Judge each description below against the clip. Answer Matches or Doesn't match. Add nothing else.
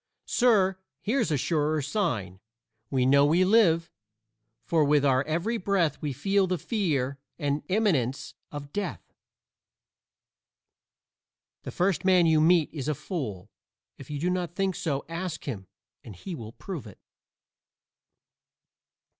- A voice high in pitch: Doesn't match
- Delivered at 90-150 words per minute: Matches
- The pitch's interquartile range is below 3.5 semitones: Doesn't match